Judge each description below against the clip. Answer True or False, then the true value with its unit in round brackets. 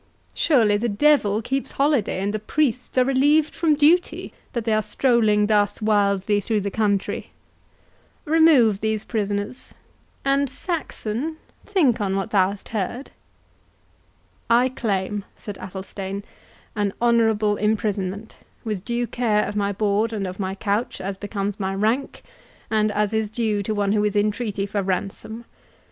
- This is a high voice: True (215 Hz)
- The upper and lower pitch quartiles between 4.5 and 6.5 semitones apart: False (3.0 semitones)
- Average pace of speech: True (150 wpm)